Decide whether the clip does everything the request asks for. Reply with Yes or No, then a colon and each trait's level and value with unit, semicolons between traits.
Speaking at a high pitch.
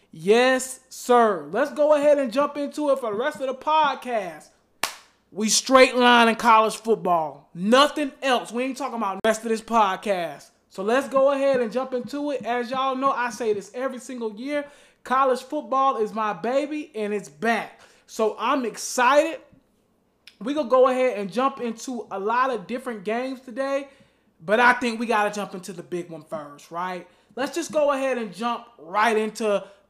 Yes: high, 245 Hz